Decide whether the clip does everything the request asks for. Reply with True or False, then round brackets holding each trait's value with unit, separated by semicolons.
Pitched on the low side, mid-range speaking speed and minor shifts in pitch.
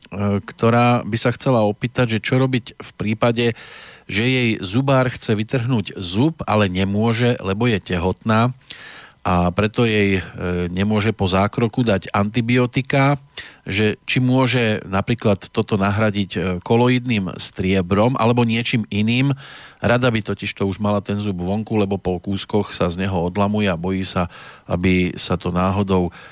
False (105 Hz; 145 wpm; 3.8 semitones)